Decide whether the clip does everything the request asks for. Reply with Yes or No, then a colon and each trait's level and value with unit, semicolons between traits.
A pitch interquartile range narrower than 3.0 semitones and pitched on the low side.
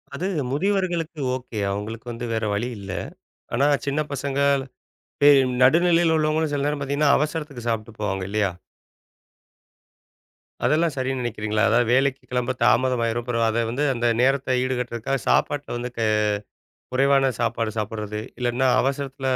No: average, 3.5 semitones; low, 130 Hz